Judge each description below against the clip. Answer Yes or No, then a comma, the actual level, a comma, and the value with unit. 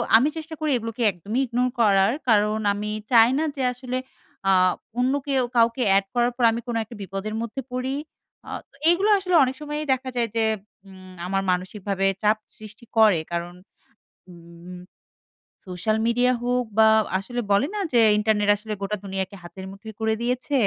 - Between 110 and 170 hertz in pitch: No, high, 220 Hz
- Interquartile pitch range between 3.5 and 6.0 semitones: Yes, average, 4.2 semitones